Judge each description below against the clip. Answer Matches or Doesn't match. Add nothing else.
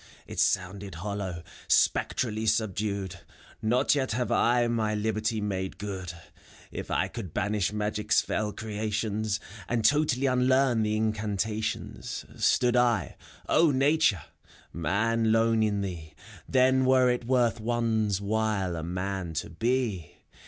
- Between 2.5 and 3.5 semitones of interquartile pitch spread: Matches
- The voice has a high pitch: Doesn't match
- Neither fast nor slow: Doesn't match